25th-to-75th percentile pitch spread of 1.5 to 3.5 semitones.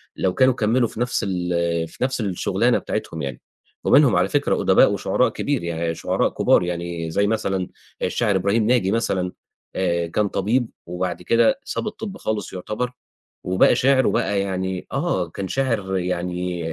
No: average, 4.5 semitones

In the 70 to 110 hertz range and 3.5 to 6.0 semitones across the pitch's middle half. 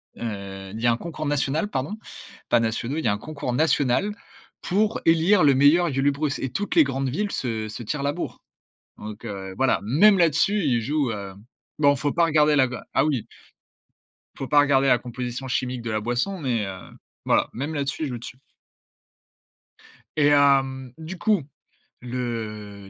No: low, 135 Hz; average, 4.6 semitones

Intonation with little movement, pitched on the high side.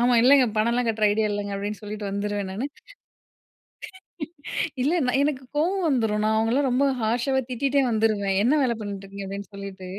No: average, 4.1 semitones; high, 220 Hz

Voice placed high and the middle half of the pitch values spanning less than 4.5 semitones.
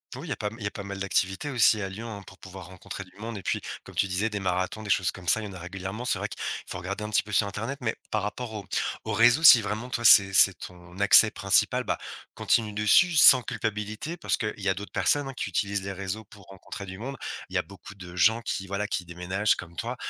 No: low, 100 Hz; average, 2.8 semitones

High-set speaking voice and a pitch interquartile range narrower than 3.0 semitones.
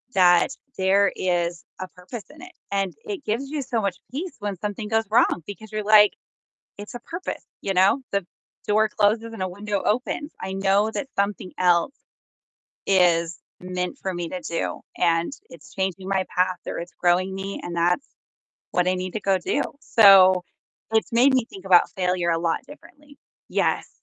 No: high, 195 Hz; average, 3.3 semitones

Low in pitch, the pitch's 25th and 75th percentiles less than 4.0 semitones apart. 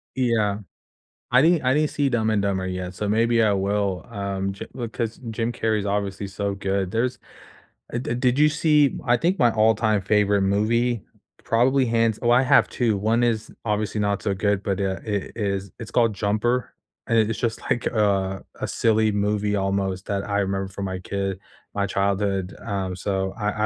Yes: low, 105 Hz; average, 3.0 semitones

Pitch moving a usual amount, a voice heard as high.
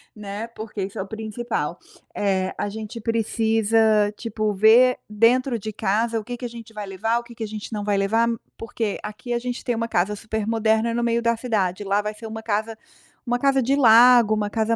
No: narrow, 1.9 semitones; high, 220 Hz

